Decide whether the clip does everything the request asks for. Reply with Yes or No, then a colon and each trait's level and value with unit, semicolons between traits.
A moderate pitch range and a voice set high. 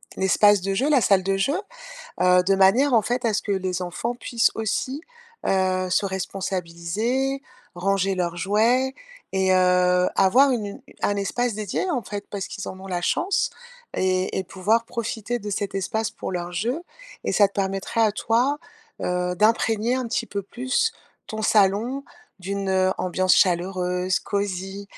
Yes: average, 3.6 semitones; high, 195 Hz